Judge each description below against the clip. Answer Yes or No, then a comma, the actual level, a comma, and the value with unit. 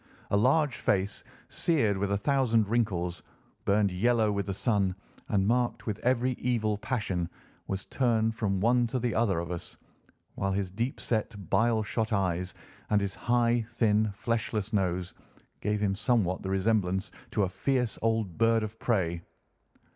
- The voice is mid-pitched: No, low, 105 Hz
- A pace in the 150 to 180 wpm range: Yes, average, 160 wpm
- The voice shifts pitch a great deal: No, average, 3.3 semitones